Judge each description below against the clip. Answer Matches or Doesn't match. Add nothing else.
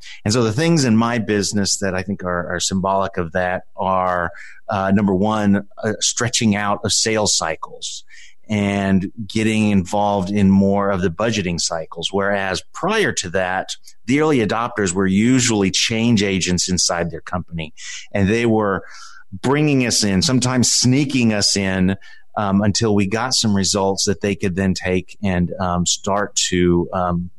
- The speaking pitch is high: Doesn't match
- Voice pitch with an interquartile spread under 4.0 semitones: Matches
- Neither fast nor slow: Matches